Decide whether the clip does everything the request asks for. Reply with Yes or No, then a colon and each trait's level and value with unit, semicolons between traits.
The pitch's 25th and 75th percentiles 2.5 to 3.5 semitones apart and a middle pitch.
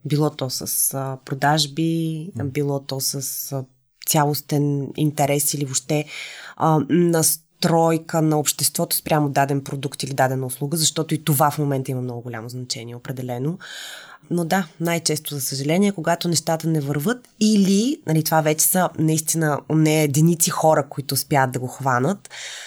Yes: average, 2.8 semitones; medium, 150 Hz